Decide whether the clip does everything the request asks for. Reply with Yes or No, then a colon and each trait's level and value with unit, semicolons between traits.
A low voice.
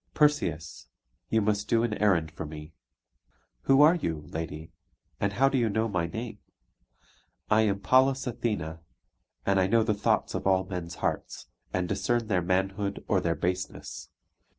Yes: low, 100 Hz